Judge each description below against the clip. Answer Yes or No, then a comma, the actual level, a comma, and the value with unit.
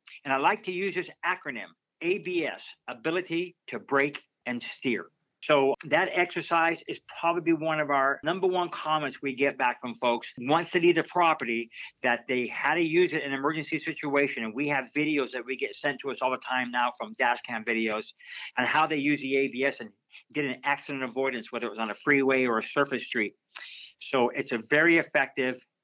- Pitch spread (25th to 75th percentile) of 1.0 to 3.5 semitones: No, average, 4.2 semitones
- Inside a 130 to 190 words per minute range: No, average, 200 wpm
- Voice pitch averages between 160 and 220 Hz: No, medium, 140 Hz